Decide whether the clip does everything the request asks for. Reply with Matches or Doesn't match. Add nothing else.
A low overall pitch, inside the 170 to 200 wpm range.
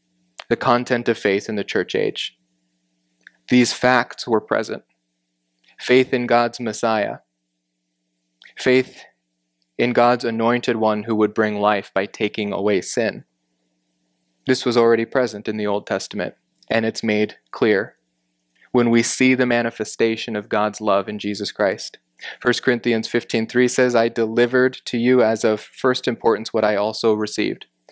Doesn't match